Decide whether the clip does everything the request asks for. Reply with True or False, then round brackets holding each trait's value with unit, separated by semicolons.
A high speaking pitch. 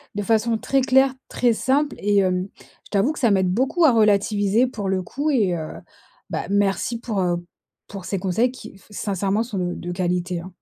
True (205 Hz)